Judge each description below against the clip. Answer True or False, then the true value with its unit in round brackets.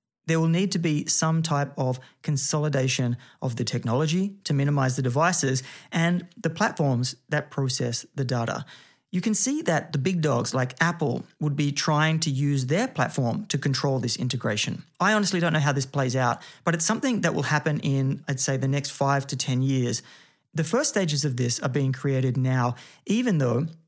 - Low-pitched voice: False (145 Hz)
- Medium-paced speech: True (195 wpm)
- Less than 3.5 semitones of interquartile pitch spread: False (4.0 semitones)